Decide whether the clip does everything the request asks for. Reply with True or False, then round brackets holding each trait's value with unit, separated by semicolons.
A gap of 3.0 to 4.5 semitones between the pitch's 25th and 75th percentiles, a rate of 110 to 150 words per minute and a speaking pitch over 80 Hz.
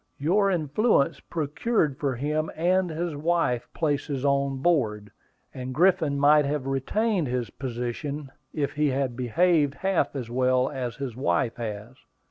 True (4.0 semitones; 140 wpm; 140 Hz)